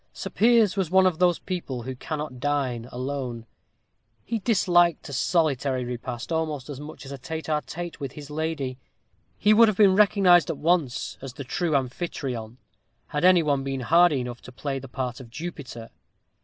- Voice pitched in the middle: Yes, medium, 145 Hz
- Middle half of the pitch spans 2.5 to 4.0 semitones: No, average, 5.2 semitones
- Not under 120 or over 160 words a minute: No, average, 185 wpm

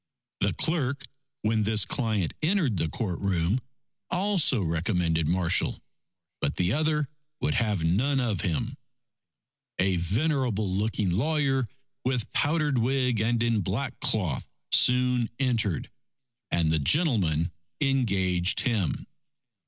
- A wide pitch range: Yes, wide, 6.5 semitones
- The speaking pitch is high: No, low, 110 Hz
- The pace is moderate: No, slow, 115 wpm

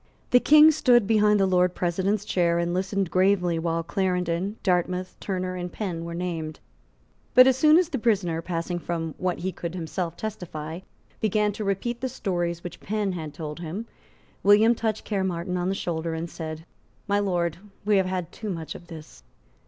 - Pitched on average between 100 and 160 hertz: No, medium, 180 Hz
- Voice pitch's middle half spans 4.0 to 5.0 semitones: No, average, 3.3 semitones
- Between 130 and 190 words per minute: Yes, average, 180 wpm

